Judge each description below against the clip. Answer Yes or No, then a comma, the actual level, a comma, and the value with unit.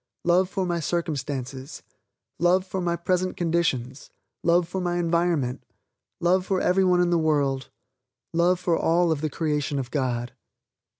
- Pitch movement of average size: Yes, average, 3.6 semitones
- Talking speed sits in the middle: Yes, average, 155 wpm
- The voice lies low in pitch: No, medium, 170 Hz